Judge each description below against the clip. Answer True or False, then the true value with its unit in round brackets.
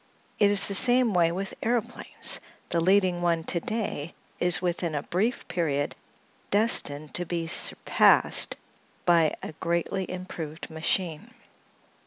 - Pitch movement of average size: True (3.2 semitones)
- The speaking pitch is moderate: True (175 Hz)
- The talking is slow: True (130 wpm)